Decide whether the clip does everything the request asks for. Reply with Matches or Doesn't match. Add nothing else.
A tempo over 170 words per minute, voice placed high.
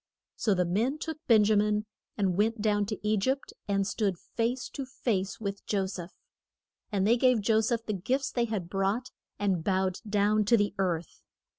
Matches